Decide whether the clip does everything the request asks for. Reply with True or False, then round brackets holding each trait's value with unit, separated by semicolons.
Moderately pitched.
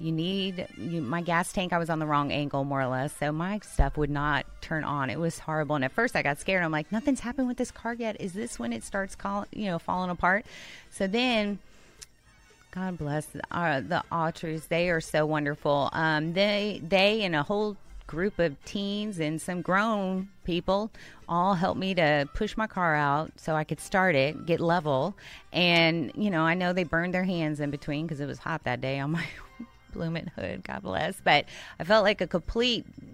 True (170 Hz)